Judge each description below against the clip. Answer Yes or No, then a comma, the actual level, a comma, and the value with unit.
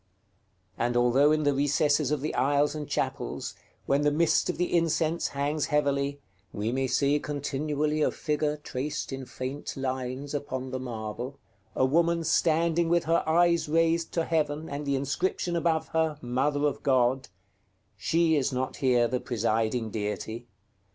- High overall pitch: No, medium, 145 Hz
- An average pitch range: Yes, average, 3.1 semitones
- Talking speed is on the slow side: No, average, 160 wpm